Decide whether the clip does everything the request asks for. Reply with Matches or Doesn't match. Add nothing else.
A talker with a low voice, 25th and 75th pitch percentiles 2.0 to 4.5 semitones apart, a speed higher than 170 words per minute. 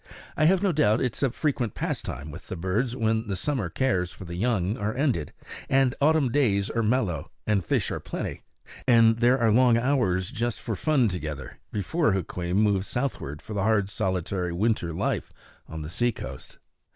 Doesn't match